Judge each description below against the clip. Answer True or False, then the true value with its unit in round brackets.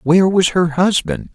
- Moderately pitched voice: True (175 Hz)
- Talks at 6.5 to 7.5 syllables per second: False (4.7 syllables/s)